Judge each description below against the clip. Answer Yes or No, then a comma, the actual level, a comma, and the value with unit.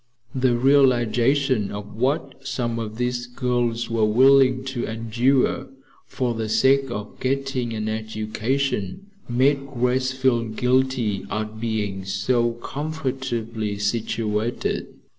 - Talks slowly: Yes, slow, 110 wpm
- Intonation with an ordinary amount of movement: Yes, average, 3.1 semitones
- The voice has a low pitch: Yes, low, 120 Hz